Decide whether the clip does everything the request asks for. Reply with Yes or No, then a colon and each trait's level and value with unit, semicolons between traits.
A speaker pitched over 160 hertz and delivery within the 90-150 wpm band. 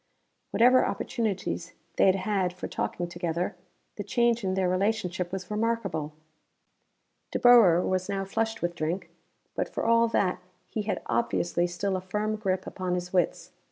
No: high, 190 Hz; average, 160 wpm